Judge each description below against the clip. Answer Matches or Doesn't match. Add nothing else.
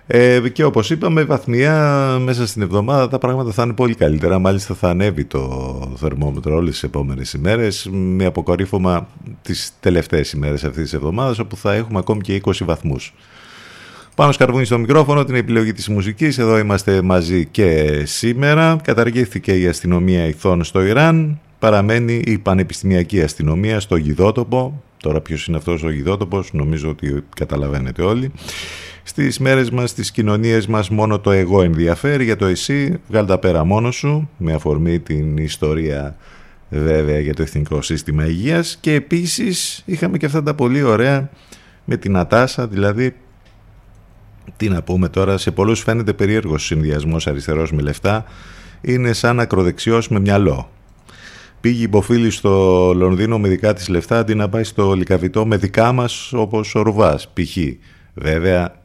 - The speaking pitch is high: Doesn't match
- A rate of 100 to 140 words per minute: Doesn't match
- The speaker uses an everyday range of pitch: Doesn't match